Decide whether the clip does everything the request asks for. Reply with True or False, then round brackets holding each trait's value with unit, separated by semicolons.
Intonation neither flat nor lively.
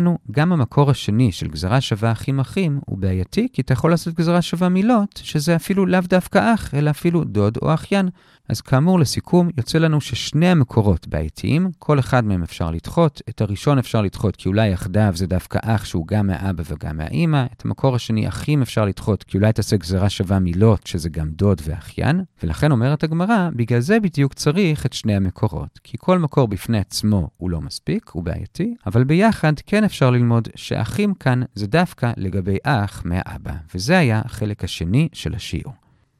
False (7.6 semitones)